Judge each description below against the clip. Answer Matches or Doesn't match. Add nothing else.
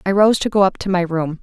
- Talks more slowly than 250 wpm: Doesn't match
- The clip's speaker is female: Matches